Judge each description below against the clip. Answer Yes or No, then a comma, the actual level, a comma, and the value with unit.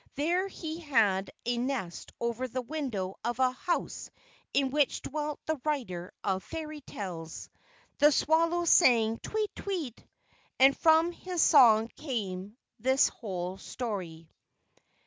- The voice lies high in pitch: Yes, very high, 255 Hz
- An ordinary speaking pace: No, slow, 125 wpm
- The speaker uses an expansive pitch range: Yes, wide, 7.1 semitones